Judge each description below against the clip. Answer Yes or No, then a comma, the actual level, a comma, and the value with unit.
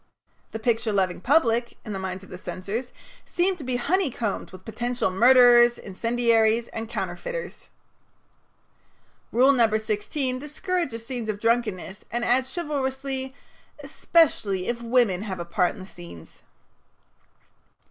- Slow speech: Yes, slow, 130 wpm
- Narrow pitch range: No, average, 4.2 semitones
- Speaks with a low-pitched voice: No, high, 235 Hz